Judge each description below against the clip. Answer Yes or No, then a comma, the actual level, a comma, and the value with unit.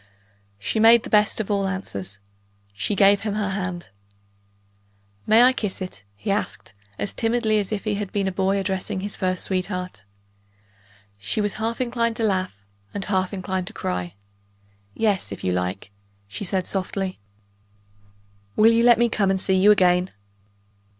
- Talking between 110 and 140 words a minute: No, average, 165 wpm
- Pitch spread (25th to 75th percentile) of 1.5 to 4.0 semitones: Yes, narrow, 2.6 semitones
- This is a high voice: Yes, high, 195 Hz